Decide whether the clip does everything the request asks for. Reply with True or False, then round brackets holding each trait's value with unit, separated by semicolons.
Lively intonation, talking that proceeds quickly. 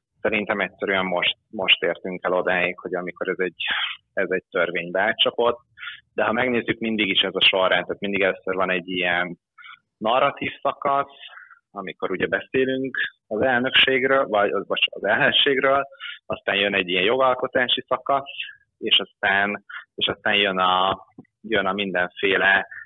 False (5.9 semitones; 145 wpm)